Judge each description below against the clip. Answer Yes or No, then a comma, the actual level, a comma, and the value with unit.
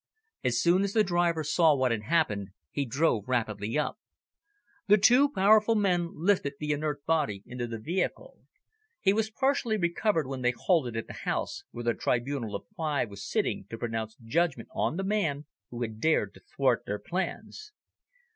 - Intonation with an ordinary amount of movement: No, wide, 8.2 semitones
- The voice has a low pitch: No, medium, 150 Hz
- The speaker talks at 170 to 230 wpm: Yes, average, 175 wpm